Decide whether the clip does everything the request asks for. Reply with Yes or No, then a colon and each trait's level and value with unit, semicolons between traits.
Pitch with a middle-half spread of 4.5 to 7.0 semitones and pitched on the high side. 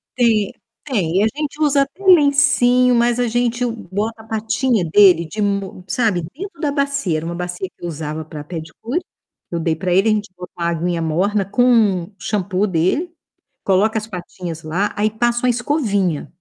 Yes: wide, 5.6 semitones; high, 210 Hz